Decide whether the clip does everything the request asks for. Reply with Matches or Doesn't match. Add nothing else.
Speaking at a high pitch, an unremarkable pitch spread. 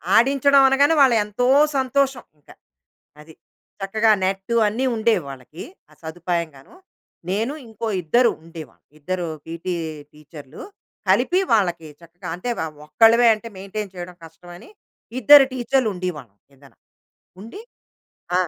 Doesn't match